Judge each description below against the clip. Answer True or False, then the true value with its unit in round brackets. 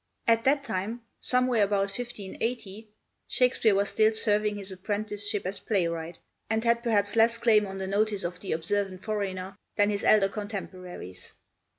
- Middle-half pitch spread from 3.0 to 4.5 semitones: False (2.5 semitones)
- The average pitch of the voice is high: True (205 Hz)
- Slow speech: False (155 wpm)